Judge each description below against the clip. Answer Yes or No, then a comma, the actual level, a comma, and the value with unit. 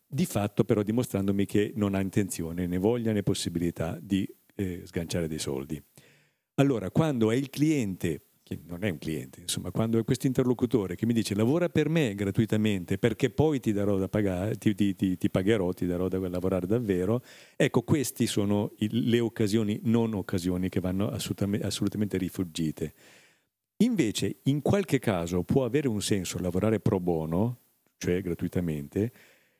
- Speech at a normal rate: Yes, average, 160 wpm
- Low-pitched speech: Yes, low, 105 Hz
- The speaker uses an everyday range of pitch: Yes, average, 4.1 semitones